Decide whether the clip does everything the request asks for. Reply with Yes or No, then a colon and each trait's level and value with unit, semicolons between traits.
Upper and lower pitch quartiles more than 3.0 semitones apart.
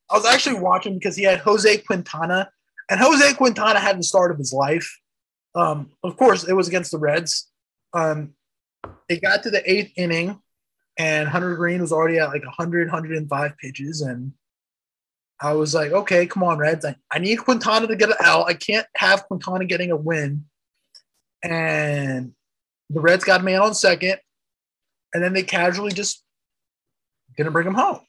Yes: average, 4.8 semitones